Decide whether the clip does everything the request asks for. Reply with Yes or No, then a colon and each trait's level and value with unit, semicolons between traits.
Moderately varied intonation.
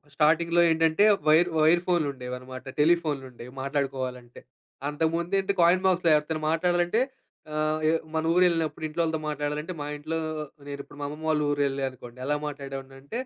Yes: average, 3.5 semitones